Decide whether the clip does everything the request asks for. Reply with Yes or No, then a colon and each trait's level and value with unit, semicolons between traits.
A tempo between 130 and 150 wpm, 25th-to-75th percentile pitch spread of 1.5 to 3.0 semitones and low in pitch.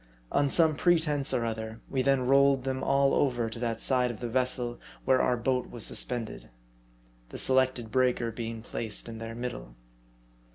No: average, 170 wpm; narrow, 2.6 semitones; low, 125 Hz